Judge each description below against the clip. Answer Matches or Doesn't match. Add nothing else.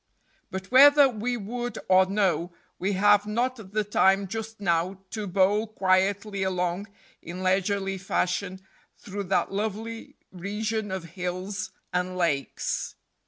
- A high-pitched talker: Matches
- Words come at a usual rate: Doesn't match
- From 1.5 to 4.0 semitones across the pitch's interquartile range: Matches